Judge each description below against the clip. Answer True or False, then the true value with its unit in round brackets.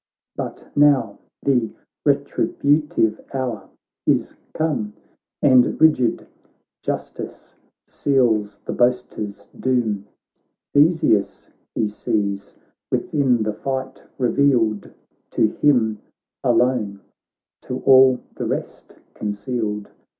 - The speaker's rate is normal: False (85 wpm)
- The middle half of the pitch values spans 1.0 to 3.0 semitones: False (4.0 semitones)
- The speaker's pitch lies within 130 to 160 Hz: False (120 Hz)